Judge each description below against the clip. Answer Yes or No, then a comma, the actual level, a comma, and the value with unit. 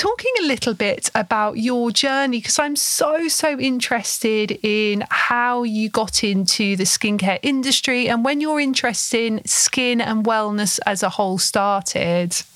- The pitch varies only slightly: No, average, 4.1 semitones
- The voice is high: Yes, high, 230 Hz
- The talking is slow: No, average, 155 wpm